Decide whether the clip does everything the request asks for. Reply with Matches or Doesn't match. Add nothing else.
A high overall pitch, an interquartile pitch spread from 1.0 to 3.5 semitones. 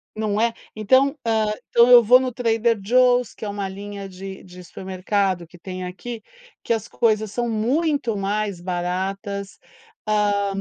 Matches